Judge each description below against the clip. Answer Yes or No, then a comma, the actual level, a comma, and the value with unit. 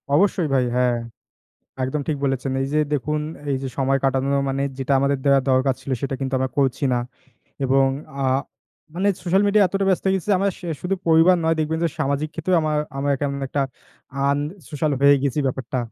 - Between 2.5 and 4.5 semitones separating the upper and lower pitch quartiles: Yes, average, 3.2 semitones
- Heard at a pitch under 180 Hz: Yes, medium, 140 Hz